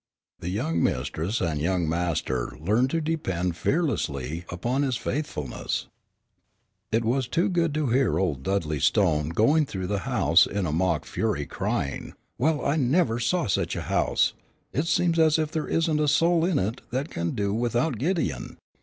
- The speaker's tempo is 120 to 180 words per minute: Yes, average, 165 wpm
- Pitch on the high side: No, low, 115 Hz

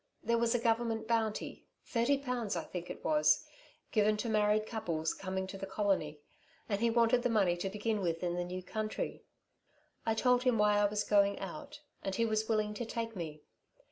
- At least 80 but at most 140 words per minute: No, average, 200 wpm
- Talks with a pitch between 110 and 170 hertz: No, high, 210 Hz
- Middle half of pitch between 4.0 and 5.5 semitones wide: No, average, 3.3 semitones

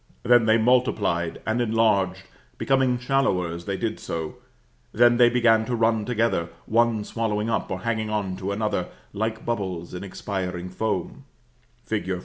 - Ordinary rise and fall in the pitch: Yes, average, 3.8 semitones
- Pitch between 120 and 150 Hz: No, low, 110 Hz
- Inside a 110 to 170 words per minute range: Yes, average, 150 wpm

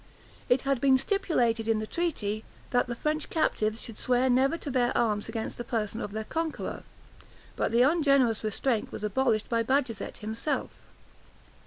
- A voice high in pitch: Yes, high, 240 Hz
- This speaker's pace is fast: No, average, 165 wpm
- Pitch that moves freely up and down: No, average, 3.8 semitones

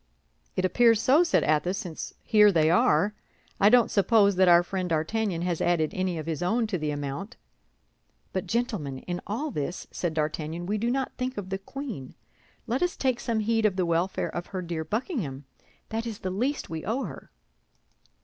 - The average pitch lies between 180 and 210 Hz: Yes, high, 190 Hz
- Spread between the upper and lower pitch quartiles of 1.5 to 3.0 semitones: No, average, 5.3 semitones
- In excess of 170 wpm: Yes, average, 190 wpm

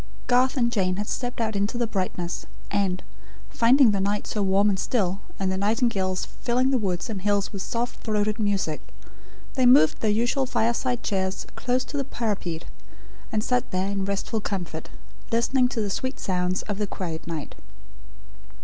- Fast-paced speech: No, average, 175 wpm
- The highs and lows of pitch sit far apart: No, average, 3.9 semitones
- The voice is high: Yes, high, 205 Hz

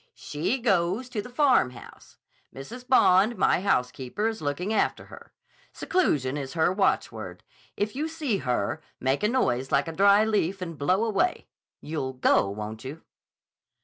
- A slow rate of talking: No, average, 150 wpm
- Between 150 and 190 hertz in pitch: Yes, medium, 185 Hz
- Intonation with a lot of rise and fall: Yes, wide, 8.4 semitones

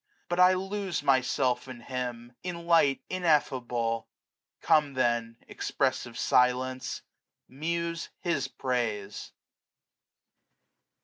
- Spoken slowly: Yes, slow, 85 wpm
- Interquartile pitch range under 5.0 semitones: No, wide, 5.6 semitones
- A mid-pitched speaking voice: No, low, 130 Hz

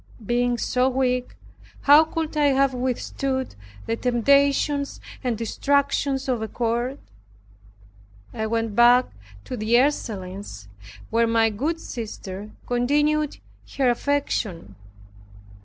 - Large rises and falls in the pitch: No, average, 3.5 semitones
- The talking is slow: Yes, slow, 105 wpm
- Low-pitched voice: No, very high, 250 Hz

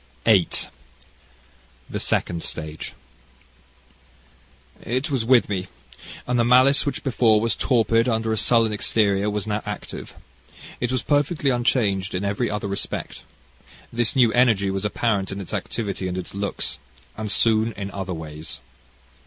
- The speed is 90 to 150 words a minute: Yes, average, 145 wpm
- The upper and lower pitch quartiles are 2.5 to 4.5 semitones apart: Yes, average, 3.5 semitones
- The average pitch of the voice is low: Yes, low, 110 Hz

